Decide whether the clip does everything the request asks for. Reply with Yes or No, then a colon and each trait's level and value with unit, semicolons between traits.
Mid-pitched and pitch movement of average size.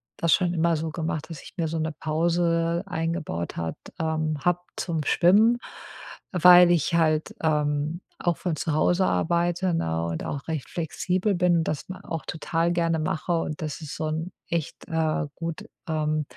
No: medium, 165 Hz; narrow, 1.9 semitones